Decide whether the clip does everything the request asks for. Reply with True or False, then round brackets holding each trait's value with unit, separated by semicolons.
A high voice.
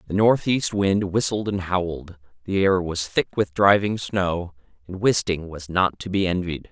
False (95 Hz)